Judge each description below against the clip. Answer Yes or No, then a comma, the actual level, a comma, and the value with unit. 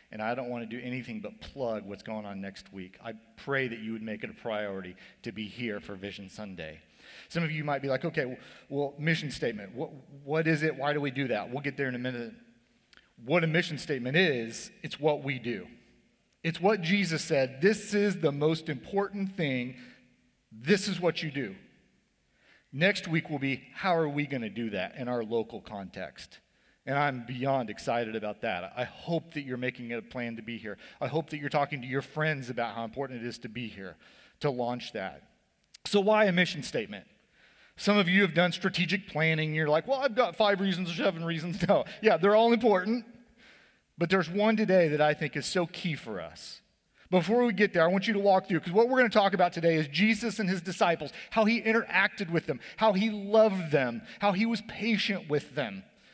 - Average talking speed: No, fast, 220 wpm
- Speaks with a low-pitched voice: No, medium, 155 Hz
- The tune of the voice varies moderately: No, wide, 8.0 semitones